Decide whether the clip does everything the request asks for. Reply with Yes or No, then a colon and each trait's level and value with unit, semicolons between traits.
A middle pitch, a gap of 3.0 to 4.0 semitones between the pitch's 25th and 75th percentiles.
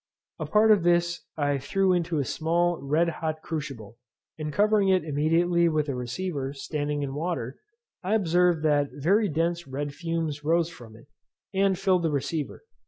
Yes: medium, 165 Hz; average, 3.4 semitones